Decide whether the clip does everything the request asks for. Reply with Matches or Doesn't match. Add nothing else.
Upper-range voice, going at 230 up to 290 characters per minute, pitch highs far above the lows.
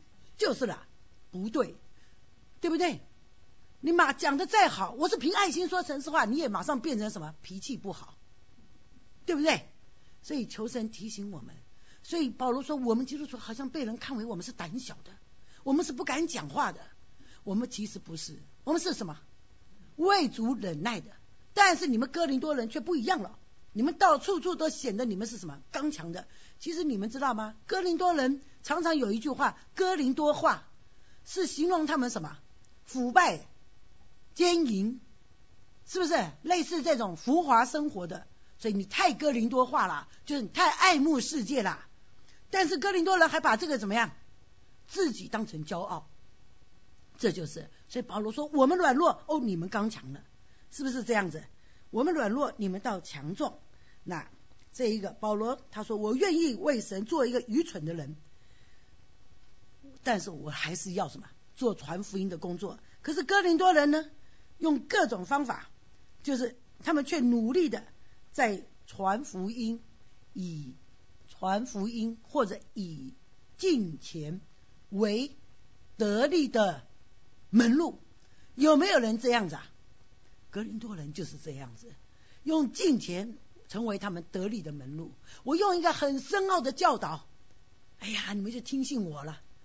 Matches